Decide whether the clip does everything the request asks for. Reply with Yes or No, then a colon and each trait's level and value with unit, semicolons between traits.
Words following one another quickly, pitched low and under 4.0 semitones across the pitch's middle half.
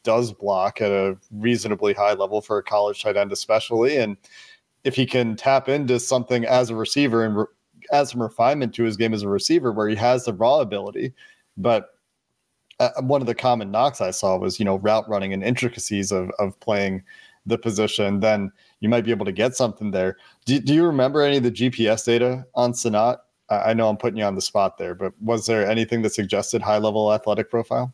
Yes: fast, 215 wpm; low, 115 Hz; average, 2.9 semitones